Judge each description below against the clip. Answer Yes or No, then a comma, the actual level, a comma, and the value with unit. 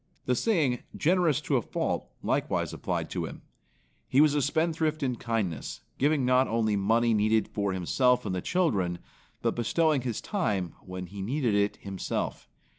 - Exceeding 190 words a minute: No, average, 165 wpm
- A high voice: No, low, 120 Hz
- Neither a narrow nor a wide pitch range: No, wide, 6.6 semitones